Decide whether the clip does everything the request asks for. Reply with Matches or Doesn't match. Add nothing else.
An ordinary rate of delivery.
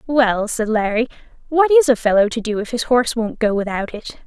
Doesn't match